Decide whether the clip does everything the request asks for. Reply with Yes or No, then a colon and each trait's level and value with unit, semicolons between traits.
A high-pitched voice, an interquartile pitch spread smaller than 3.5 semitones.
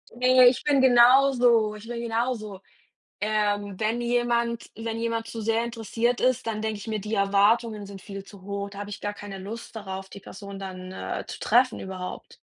Yes: high, 220 Hz; average, 2.9 semitones